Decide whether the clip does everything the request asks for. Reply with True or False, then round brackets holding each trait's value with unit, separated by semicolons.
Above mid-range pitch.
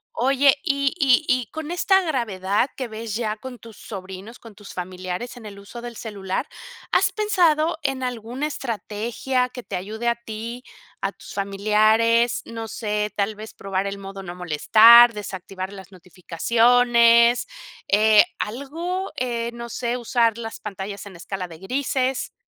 True (230 Hz)